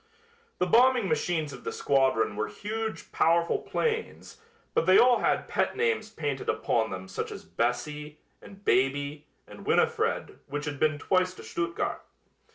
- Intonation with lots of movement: Yes, wide, 6.1 semitones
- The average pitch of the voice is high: No, medium, 155 Hz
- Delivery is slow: No, average, 155 wpm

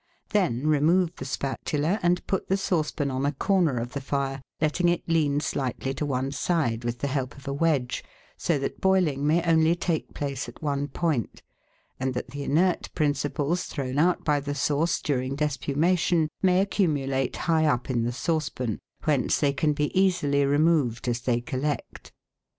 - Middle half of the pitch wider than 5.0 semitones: No, average, 3.7 semitones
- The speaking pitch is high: No, medium, 145 Hz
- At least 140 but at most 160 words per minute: No, average, 180 wpm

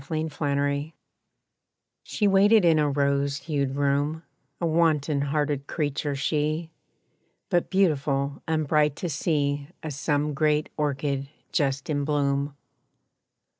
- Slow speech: Yes, slow, 115 wpm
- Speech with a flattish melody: Yes, narrow, 1.9 semitones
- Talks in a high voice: No, medium, 145 Hz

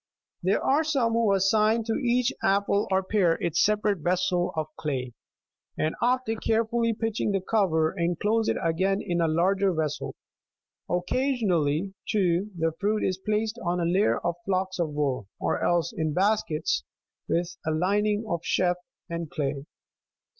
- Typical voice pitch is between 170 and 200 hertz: Yes, high, 190 Hz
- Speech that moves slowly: No, average, 160 wpm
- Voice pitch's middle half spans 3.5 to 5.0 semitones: Yes, average, 4.2 semitones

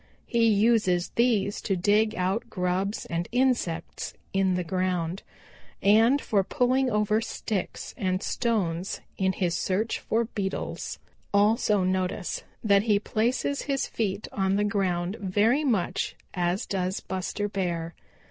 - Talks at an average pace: No, slow, 130 wpm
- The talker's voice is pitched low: No, high, 200 Hz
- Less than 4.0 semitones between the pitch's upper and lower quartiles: Yes, average, 3.3 semitones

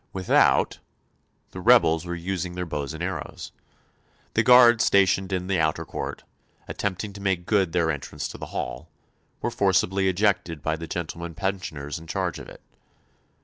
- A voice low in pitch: Yes, very low, 90 Hz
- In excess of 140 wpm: Yes, average, 160 wpm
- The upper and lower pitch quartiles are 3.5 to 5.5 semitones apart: No, average, 2.9 semitones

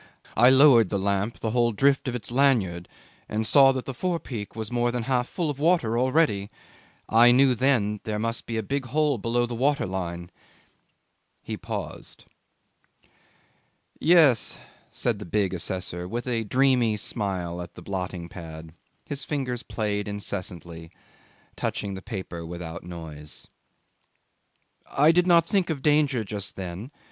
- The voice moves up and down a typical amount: No, wide, 5.9 semitones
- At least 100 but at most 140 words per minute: No, average, 155 wpm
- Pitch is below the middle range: Yes, low, 115 Hz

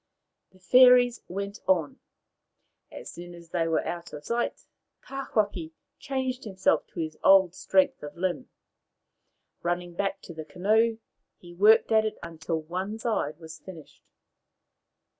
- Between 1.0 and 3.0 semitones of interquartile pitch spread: No, average, 4.4 semitones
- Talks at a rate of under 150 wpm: Yes, average, 140 wpm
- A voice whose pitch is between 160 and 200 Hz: Yes, medium, 185 Hz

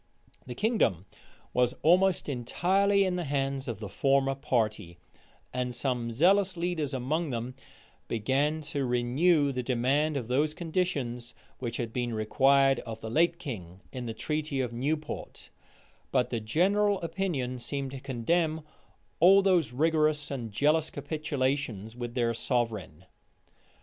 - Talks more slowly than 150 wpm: Yes, average, 140 wpm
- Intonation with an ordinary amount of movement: Yes, average, 4.7 semitones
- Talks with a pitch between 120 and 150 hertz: Yes, low, 135 Hz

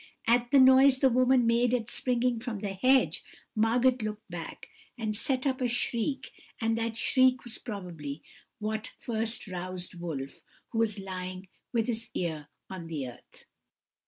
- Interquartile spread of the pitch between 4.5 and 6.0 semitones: Yes, average, 5.0 semitones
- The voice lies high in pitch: Yes, high, 225 Hz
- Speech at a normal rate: Yes, average, 160 wpm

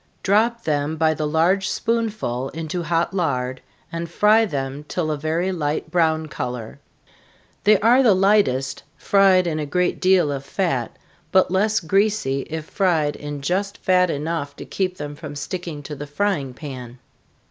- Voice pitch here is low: No, medium, 165 Hz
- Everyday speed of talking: Yes, average, 160 wpm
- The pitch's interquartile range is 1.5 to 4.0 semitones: No, average, 4.7 semitones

